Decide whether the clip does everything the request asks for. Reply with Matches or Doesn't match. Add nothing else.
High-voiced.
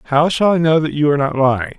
Doesn't match